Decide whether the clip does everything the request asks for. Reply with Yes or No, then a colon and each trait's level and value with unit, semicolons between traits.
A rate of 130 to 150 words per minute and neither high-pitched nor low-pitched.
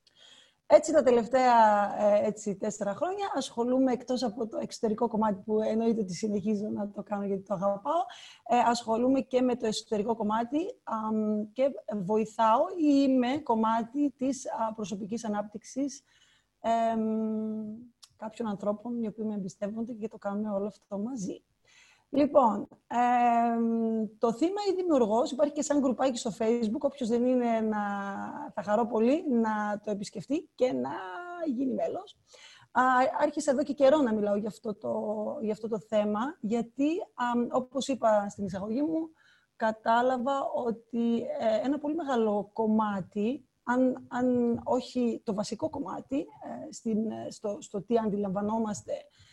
No: average, 140 wpm; high, 230 Hz